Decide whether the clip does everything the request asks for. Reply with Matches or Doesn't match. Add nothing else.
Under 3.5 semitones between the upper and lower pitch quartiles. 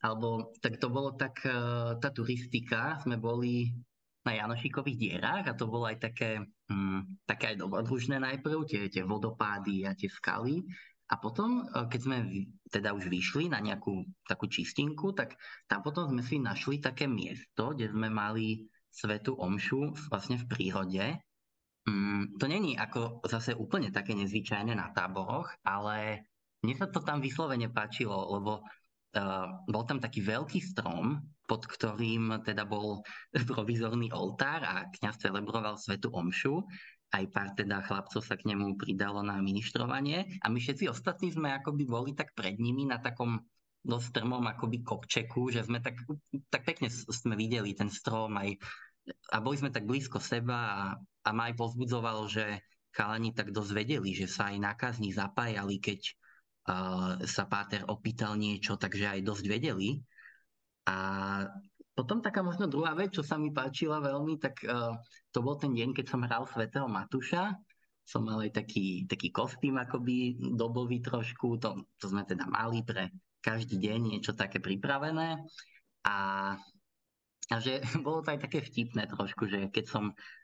Doesn't match